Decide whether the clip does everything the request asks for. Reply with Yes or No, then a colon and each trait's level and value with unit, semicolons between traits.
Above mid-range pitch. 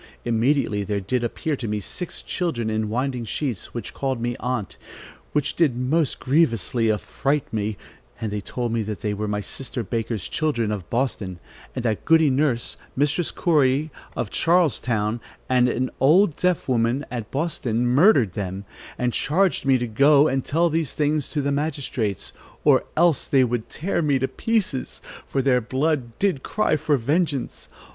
No: low, 130 Hz